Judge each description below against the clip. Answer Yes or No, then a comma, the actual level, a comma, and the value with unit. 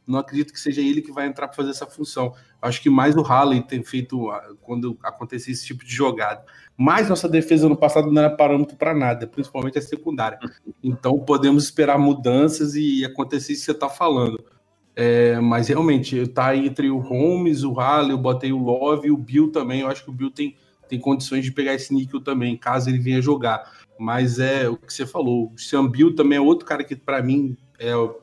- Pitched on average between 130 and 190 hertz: Yes, low, 135 Hz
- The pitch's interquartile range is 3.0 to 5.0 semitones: No, narrow, 2.6 semitones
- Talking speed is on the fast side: Yes, fast, 215 wpm